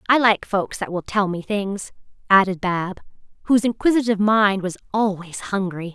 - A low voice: No, high, 200 Hz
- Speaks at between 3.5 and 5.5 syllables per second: Yes, 5.0 syllables/s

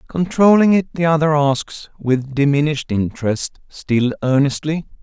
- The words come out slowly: Yes, slow, 120 wpm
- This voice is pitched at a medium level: Yes, medium, 145 Hz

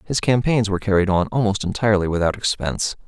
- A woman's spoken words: No, male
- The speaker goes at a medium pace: Yes, average, 175 wpm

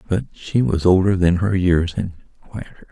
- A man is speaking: Yes, male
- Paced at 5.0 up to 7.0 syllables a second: No, 4.8 syllables/s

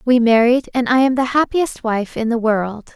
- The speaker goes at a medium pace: No, fast, 225 wpm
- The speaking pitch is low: No, high, 240 Hz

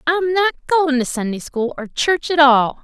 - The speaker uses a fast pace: Yes, fast, 210 wpm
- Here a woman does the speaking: Yes, female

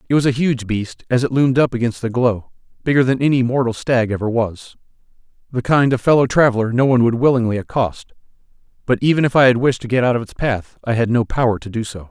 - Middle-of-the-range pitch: No, low, 125 Hz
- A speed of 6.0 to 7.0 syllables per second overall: Yes, 6.3 syllables/s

